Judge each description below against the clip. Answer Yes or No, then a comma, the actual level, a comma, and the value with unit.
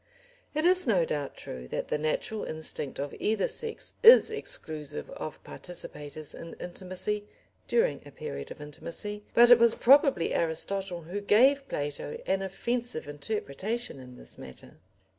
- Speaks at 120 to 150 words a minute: Yes, average, 145 wpm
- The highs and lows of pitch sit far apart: Yes, wide, 7.8 semitones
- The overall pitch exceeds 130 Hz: Yes, high, 190 Hz